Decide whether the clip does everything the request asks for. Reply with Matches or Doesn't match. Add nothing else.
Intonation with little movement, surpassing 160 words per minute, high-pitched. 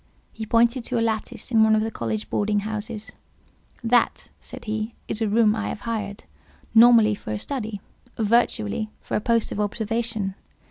Matches